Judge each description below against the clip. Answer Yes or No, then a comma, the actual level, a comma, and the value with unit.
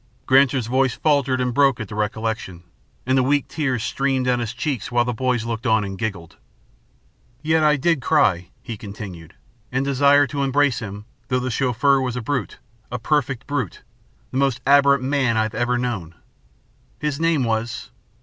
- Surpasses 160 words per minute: Yes, average, 180 wpm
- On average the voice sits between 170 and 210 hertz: No, low, 125 Hz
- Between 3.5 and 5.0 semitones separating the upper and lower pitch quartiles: Yes, average, 3.8 semitones